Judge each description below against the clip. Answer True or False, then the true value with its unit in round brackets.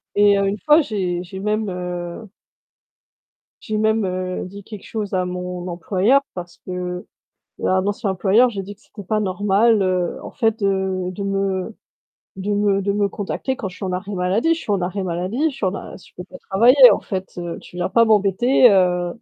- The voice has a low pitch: False (195 Hz)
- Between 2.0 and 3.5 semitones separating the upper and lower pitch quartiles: True (2.7 semitones)